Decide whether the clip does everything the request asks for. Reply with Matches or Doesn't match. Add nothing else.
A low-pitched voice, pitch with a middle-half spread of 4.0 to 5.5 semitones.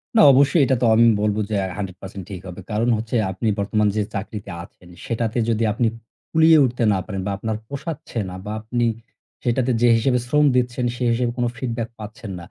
Doesn't match